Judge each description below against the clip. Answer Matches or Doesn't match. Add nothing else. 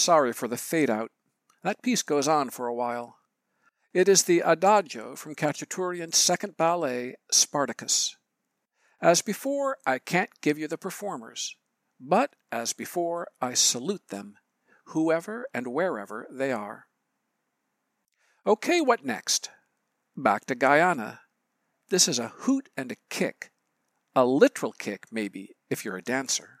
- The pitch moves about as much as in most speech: Doesn't match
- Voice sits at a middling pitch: Matches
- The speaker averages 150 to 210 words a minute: Doesn't match